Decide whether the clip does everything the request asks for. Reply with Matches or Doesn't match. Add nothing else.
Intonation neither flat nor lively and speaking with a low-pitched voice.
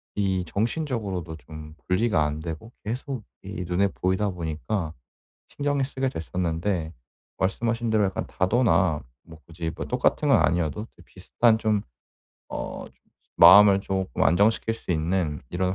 Matches